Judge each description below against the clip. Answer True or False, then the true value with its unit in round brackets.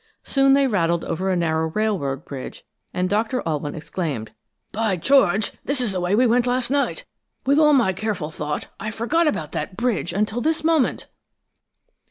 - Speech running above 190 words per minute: False (175 wpm)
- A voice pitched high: True (210 Hz)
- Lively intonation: True (7.2 semitones)